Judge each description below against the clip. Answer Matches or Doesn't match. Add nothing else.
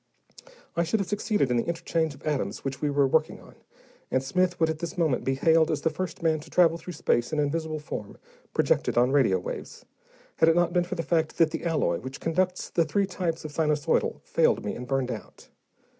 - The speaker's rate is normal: Doesn't match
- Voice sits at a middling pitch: Matches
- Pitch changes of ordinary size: Matches